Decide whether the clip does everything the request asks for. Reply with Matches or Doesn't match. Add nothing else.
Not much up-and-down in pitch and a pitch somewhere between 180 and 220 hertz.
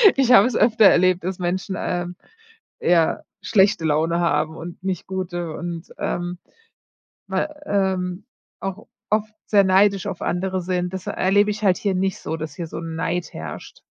Matches